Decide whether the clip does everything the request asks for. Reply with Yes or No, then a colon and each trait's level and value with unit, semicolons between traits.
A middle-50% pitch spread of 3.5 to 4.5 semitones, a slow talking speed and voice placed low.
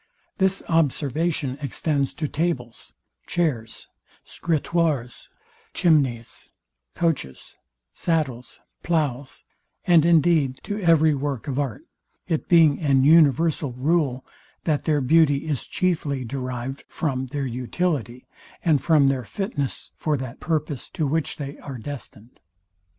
No: average, 3.9 semitones; slow, 115 wpm; medium, 145 Hz